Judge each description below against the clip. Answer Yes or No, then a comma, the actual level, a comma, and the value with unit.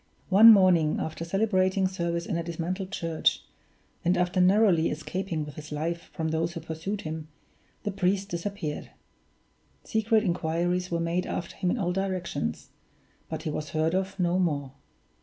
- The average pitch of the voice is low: No, medium, 175 Hz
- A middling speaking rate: Yes, average, 160 wpm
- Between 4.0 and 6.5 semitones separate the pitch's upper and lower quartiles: No, average, 2.8 semitones